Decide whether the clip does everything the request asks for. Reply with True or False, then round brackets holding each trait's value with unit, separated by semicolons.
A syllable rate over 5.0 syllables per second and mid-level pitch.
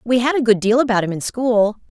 False (6.0 syllables/s; 230 Hz)